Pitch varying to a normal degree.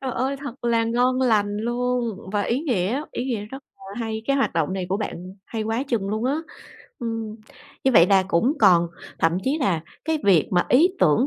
Yes: average, 4.4 semitones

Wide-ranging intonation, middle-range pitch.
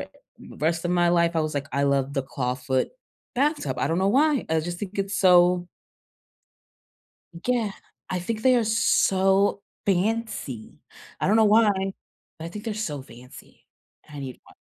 Yes: wide, 6.6 semitones; medium, 180 Hz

